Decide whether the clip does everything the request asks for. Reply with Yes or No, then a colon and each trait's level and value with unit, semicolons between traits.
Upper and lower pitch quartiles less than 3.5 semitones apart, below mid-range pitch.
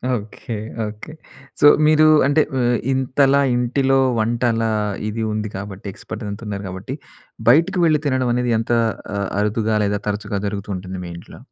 No: average, 4.3 semitones; low, 115 Hz